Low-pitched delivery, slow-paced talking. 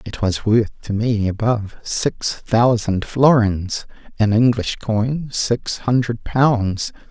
Yes: low, 115 Hz; slow, 125 wpm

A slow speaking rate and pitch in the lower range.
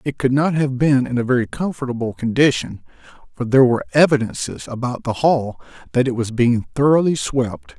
No: average, 175 wpm; low, 125 Hz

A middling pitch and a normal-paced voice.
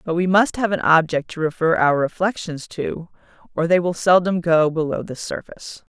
Yes: medium, 170 Hz; average, 190 wpm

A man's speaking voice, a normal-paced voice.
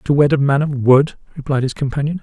No: male; fast, 245 wpm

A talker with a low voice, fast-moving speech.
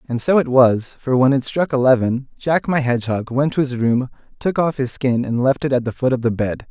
Yes: low, 130 Hz; fast, 260 wpm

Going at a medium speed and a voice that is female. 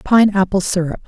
Yes: average, 165 wpm; female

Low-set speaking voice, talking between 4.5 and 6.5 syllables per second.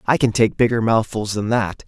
Yes: low, 110 Hz; 5.2 syllables/s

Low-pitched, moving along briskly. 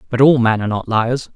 Yes: low, 120 Hz; fast, 265 wpm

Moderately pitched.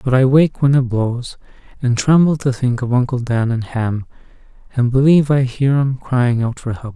No: low, 130 Hz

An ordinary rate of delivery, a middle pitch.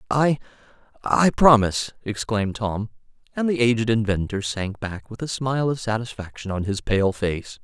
No: average, 150 wpm; low, 115 Hz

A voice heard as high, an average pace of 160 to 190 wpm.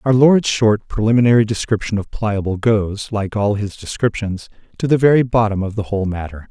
No: low, 110 Hz; average, 185 wpm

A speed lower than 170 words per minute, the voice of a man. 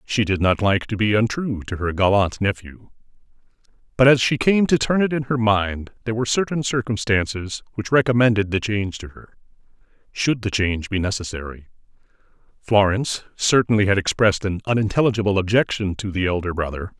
Yes: average, 160 wpm; male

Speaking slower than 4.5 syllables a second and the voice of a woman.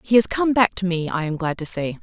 No: 5.8 syllables/s; female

